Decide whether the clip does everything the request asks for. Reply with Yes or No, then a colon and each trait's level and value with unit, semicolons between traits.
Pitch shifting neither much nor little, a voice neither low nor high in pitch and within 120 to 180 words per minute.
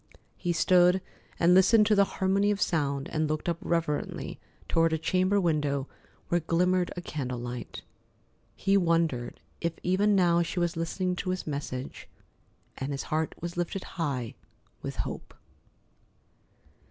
Yes: average, 3.3 semitones; medium, 170 Hz; average, 145 wpm